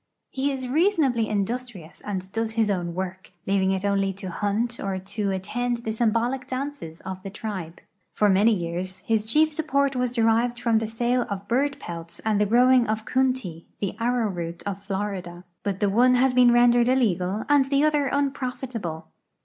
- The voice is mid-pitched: No, high, 220 Hz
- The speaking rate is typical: Yes, average, 175 wpm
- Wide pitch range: No, average, 4.7 semitones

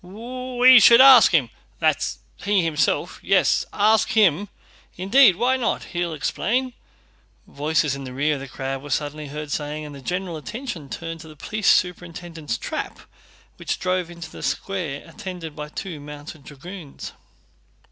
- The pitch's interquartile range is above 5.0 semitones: Yes, wide, 5.4 semitones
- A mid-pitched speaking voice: Yes, medium, 165 Hz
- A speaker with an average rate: Yes, average, 155 wpm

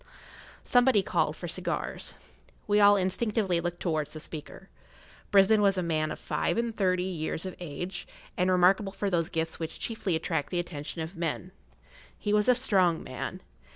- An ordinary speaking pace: Yes, average, 170 wpm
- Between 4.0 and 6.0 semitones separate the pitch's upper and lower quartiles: No, average, 3.5 semitones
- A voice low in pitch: No, medium, 185 Hz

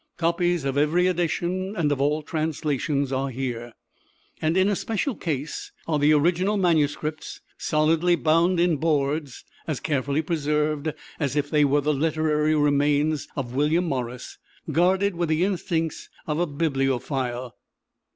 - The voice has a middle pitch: Yes, medium, 155 Hz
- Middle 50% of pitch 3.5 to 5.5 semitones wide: No, average, 3.0 semitones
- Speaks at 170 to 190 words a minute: No, slow, 135 wpm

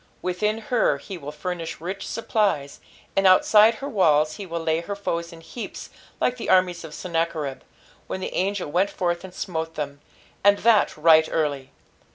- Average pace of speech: Yes, average, 175 wpm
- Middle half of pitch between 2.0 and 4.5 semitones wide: Yes, average, 3.9 semitones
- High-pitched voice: No, medium, 175 Hz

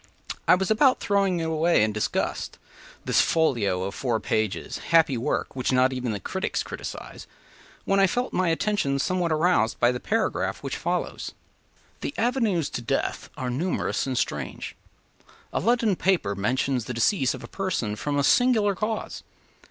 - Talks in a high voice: No, medium, 155 Hz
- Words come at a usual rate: Yes, average, 160 wpm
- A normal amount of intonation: No, wide, 7.9 semitones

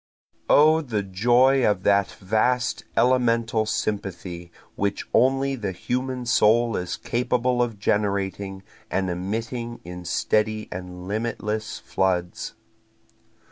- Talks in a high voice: No, low, 110 Hz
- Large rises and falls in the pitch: No, average, 4.2 semitones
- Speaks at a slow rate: Yes, slow, 105 wpm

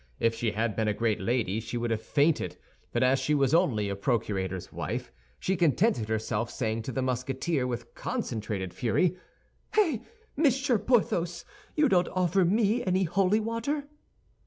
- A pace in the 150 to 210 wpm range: Yes, average, 160 wpm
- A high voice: No, low, 135 Hz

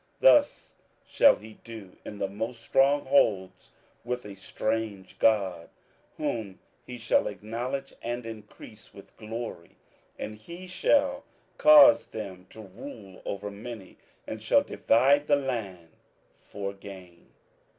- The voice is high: No, low, 110 Hz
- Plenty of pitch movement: No, average, 4.9 semitones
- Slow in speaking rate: Yes, slow, 130 wpm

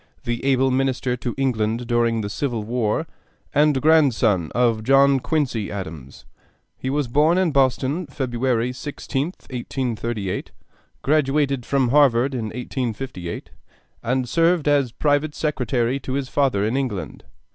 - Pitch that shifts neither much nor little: Yes, average, 3.1 semitones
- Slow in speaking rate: Yes, slow, 130 wpm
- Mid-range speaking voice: No, low, 130 Hz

